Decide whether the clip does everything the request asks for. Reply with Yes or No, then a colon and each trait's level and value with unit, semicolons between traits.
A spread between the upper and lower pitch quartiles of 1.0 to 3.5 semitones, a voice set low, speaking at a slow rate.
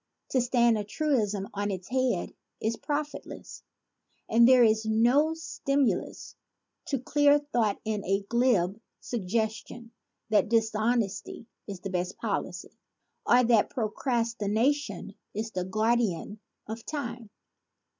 No: average, 3.2 semitones; high, 225 Hz; slow, 115 wpm